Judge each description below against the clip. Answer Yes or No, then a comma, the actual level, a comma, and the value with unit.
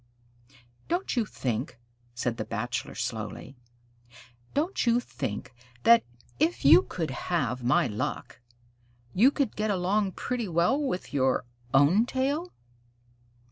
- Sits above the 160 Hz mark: Yes, medium, 185 Hz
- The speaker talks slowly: Yes, slow, 120 wpm